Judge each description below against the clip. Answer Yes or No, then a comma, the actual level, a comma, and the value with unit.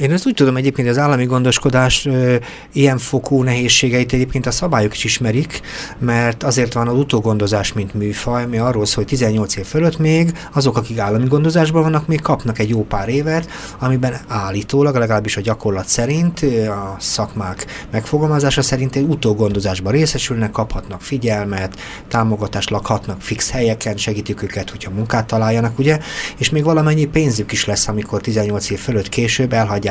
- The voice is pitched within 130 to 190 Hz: No, low, 120 Hz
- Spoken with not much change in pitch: No, average, 4.6 semitones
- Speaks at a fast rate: Yes, fast, 160 wpm